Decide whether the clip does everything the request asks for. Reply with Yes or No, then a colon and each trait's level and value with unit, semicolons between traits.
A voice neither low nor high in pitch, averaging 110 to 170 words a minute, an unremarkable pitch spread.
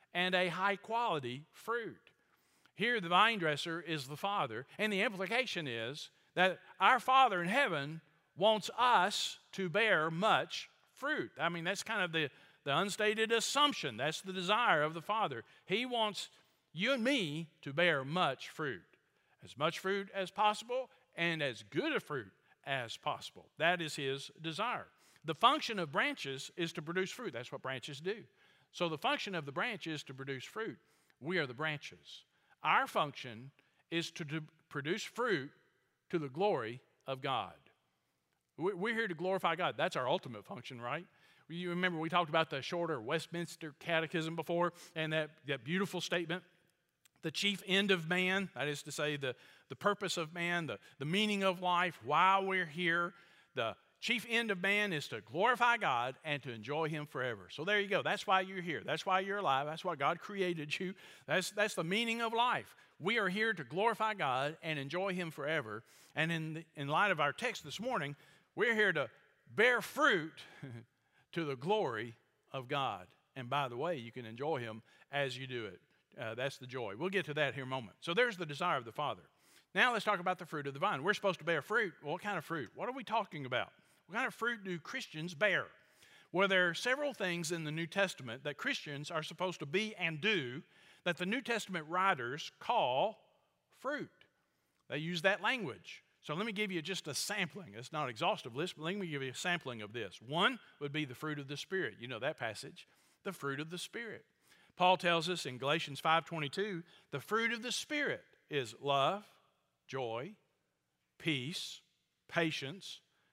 No: medium, 170 Hz; average, 190 wpm; average, 4.9 semitones